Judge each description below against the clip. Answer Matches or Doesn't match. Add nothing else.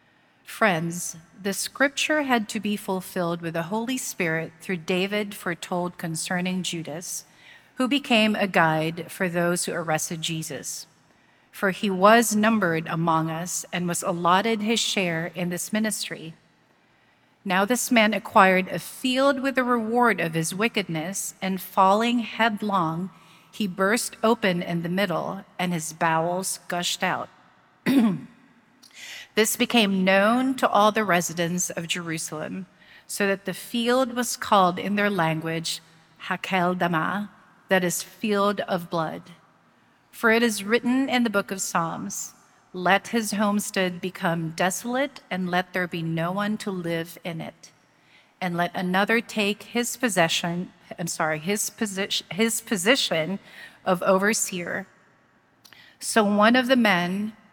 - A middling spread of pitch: Matches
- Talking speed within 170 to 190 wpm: Doesn't match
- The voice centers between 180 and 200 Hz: Matches